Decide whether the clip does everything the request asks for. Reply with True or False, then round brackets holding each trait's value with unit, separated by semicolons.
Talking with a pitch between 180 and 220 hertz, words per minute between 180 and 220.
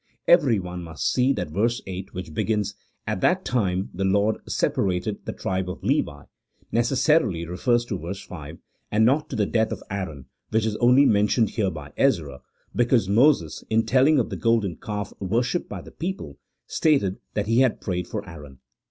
False (105 Hz; 185 wpm)